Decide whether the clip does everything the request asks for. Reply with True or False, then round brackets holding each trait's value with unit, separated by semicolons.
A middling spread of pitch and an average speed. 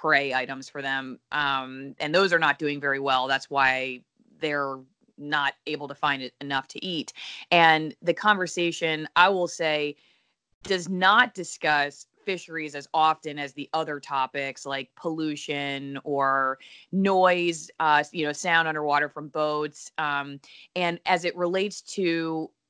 True (3.5 semitones; 150 wpm)